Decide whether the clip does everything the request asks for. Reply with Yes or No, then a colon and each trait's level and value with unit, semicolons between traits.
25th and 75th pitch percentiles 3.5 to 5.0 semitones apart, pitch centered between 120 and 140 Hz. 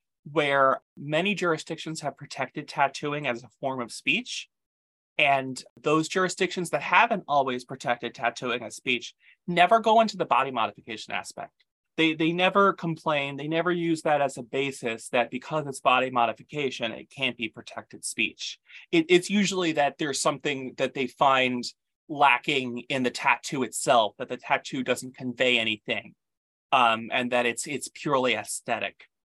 Yes: average, 4.5 semitones; low, 135 Hz